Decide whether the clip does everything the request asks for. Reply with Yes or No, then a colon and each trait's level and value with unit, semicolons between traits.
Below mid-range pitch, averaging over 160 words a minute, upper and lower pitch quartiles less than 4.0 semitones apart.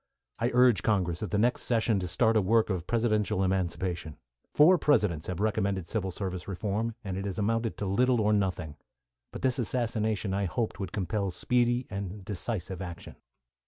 Yes: low, 100 Hz; average, 175 wpm; average, 3.5 semitones